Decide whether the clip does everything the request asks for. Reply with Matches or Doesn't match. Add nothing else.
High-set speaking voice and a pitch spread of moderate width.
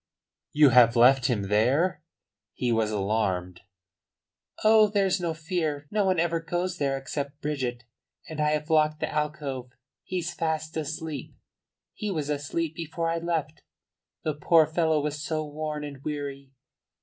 Doesn't match